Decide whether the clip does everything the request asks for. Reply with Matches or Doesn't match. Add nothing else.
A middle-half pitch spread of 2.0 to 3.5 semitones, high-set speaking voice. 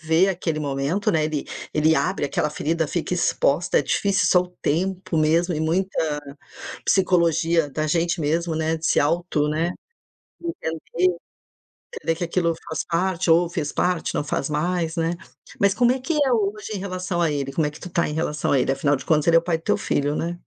Doesn't match